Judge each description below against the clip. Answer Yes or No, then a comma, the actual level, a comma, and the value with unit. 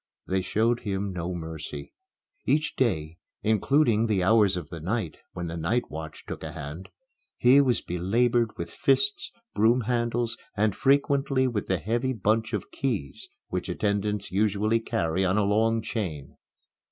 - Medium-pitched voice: No, low, 105 Hz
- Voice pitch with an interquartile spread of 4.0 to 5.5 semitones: Yes, average, 4.6 semitones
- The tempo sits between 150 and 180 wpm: Yes, average, 155 wpm